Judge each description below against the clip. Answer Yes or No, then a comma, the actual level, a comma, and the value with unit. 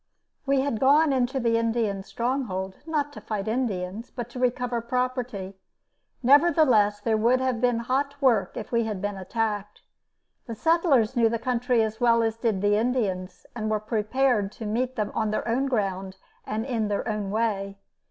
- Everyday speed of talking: Yes, average, 175 wpm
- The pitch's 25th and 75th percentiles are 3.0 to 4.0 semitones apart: Yes, average, 3.3 semitones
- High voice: Yes, high, 230 Hz